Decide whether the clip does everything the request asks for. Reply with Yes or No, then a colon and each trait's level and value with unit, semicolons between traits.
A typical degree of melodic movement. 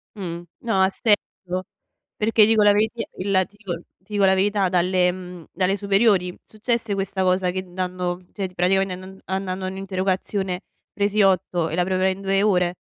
No: narrow, 1.8 semitones